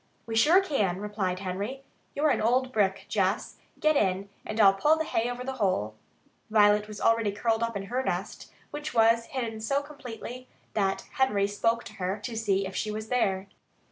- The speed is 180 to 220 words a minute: Yes, average, 190 wpm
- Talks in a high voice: Yes, high, 220 Hz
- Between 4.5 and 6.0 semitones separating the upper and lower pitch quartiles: No, average, 4.0 semitones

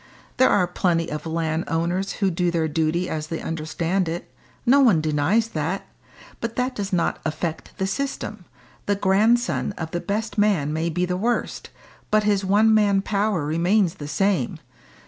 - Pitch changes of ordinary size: Yes, average, 4.3 semitones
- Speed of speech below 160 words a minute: No, average, 165 wpm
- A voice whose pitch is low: No, medium, 185 Hz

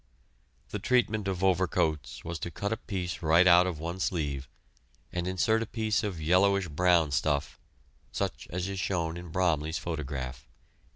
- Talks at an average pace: Yes, average, 160 wpm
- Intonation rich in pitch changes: No, average, 3.3 semitones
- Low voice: Yes, very low, 90 Hz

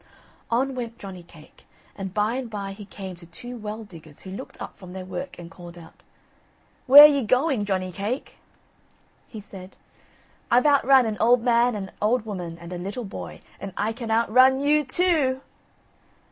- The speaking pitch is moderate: No, high, 215 Hz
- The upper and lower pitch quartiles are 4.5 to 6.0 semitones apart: Yes, average, 5.0 semitones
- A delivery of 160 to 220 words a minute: Yes, average, 190 wpm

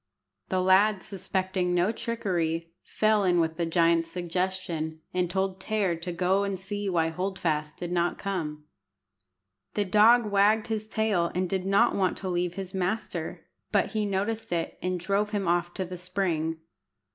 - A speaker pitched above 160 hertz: Yes, medium, 185 Hz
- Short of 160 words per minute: No, average, 170 wpm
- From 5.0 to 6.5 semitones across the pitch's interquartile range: No, narrow, 2.6 semitones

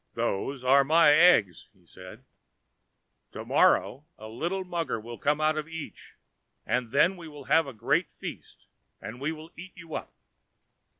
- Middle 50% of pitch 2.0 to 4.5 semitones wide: No, average, 5.0 semitones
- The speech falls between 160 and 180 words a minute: Yes, average, 165 wpm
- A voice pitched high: No, medium, 150 Hz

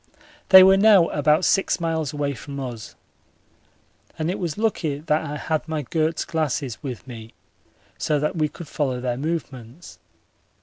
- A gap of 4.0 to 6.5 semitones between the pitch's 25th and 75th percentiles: No, average, 3.3 semitones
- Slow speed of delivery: No, average, 160 wpm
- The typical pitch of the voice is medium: Yes, medium, 150 Hz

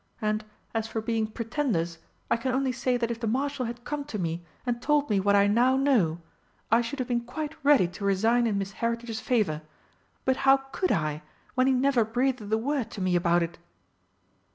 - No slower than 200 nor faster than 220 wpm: Yes, fast, 205 wpm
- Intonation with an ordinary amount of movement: Yes, average, 4.4 semitones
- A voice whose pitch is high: Yes, high, 235 Hz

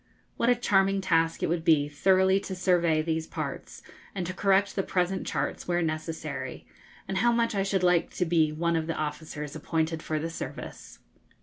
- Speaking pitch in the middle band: Yes, medium, 175 Hz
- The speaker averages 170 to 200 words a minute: Yes, average, 190 wpm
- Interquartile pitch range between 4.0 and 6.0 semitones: No, average, 3.2 semitones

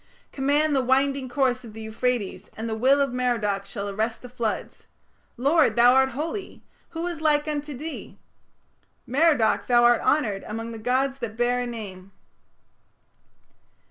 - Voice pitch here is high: Yes, very high, 250 Hz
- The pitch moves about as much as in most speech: Yes, average, 3.9 semitones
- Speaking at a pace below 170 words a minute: Yes, average, 155 wpm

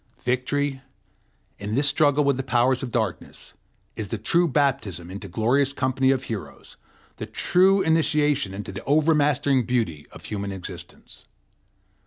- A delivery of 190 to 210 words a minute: No, average, 145 wpm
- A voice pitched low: Yes, low, 130 Hz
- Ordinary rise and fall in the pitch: Yes, average, 5.0 semitones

